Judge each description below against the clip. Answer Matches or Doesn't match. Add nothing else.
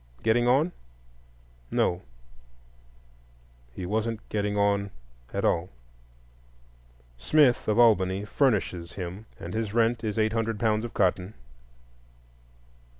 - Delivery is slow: Matches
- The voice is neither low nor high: Doesn't match